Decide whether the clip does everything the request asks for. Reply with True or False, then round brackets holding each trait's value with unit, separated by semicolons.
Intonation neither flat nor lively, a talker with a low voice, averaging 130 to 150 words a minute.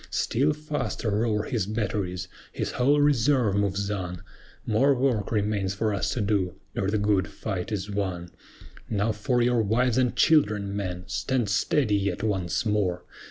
False (3.7 semitones; 105 Hz; 160 wpm)